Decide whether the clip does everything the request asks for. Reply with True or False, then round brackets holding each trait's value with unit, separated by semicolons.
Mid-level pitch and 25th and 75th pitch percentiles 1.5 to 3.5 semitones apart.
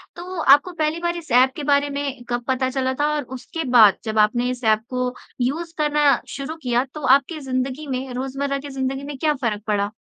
False (270 Hz; 2.9 semitones)